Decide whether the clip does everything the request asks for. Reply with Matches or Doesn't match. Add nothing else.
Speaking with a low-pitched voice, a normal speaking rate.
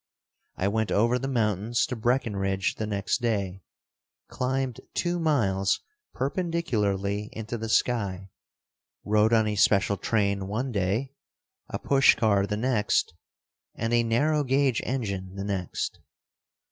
Doesn't match